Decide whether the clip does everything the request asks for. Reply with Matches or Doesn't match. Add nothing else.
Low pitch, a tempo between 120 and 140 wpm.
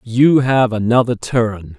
Matches